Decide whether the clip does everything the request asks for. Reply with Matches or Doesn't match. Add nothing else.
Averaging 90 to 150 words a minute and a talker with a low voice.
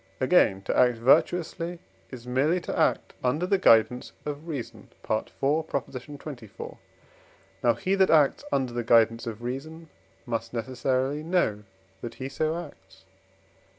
Matches